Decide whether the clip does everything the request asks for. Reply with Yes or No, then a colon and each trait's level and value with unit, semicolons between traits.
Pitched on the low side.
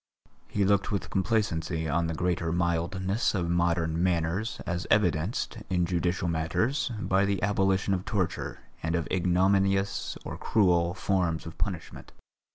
Yes: very low, 90 Hz